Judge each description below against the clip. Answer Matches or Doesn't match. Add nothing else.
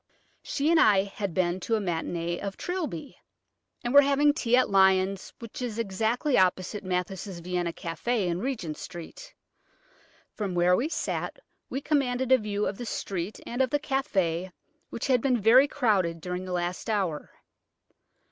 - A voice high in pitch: Matches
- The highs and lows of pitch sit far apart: Matches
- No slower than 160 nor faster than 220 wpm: Matches